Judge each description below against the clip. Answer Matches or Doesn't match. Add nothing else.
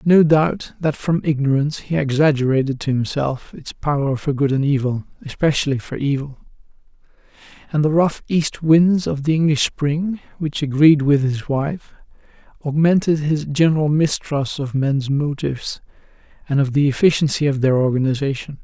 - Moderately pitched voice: Matches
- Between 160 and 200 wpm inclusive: Doesn't match